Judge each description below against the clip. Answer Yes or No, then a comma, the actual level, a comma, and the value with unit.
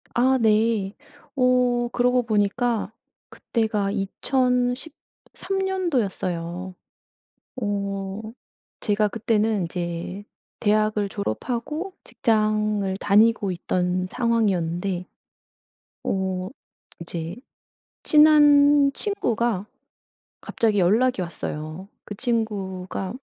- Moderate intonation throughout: Yes, average, 4.4 semitones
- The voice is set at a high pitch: Yes, high, 215 Hz